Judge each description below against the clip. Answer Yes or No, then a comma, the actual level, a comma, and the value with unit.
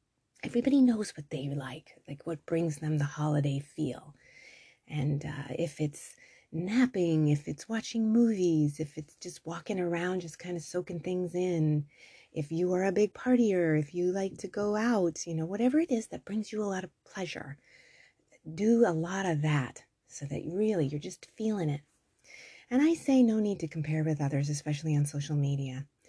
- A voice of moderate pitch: Yes, medium, 170 Hz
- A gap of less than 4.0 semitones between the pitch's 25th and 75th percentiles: No, wide, 5.5 semitones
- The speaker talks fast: No, average, 185 wpm